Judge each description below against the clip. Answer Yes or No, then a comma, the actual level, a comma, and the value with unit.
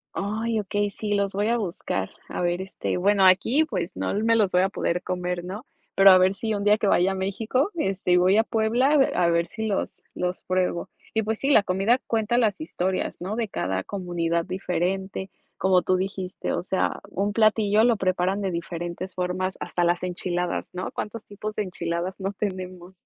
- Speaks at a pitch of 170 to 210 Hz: Yes, high, 190 Hz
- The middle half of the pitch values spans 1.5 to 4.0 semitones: Yes, average, 2.9 semitones